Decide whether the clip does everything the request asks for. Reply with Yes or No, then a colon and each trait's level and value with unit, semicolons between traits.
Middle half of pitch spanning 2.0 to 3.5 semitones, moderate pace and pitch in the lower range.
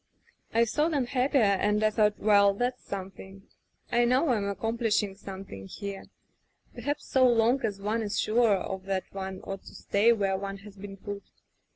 No: average, 3.1 semitones; average, 175 wpm; high, 205 Hz